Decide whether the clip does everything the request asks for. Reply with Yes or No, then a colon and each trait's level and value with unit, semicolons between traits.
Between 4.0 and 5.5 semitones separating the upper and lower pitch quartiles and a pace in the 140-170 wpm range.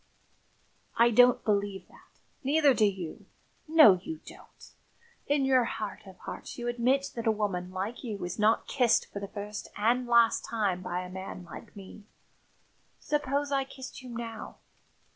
Yes: average, 4.3 semitones; average, 160 wpm